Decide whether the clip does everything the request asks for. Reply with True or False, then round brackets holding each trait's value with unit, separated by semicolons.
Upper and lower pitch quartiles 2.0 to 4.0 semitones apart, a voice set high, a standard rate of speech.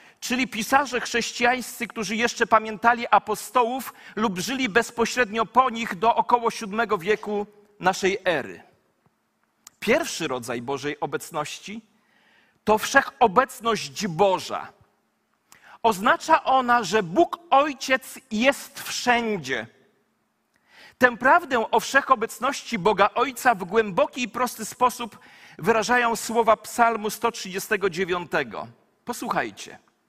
False (2.9 semitones; 230 Hz; 95 wpm)